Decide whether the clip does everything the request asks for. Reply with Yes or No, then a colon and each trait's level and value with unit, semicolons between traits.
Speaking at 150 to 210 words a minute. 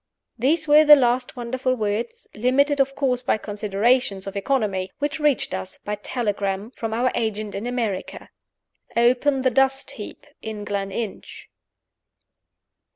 No: slow, 135 wpm